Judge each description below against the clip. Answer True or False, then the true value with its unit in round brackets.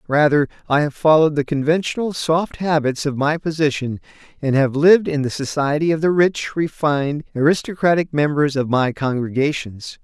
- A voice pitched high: False (150 Hz)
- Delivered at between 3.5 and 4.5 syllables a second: False (5.2 syllables/s)